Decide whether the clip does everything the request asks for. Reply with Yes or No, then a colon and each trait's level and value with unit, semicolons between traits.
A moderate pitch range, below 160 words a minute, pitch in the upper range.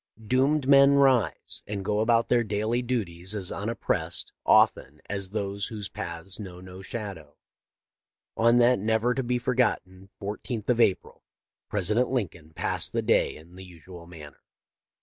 No: average, 4.5 semitones; average, 150 wpm; low, 105 Hz